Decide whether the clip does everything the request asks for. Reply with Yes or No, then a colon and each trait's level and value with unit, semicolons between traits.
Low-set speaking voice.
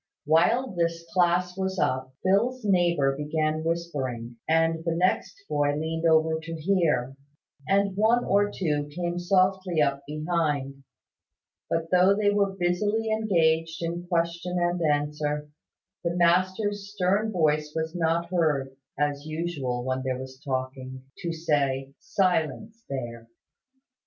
No: medium, 165 Hz